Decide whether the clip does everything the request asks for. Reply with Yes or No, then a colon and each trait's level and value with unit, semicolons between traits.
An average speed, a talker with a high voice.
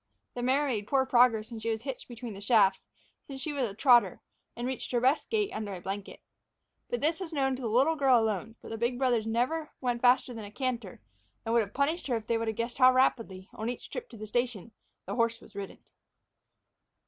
No: fast, 230 wpm; high, 240 Hz